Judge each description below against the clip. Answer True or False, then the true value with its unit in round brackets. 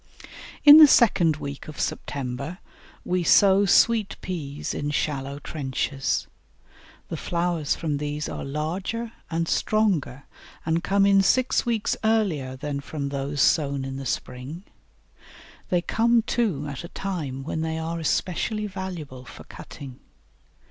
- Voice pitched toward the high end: False (160 Hz)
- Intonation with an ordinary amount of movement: False (5.7 semitones)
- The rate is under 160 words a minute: True (135 wpm)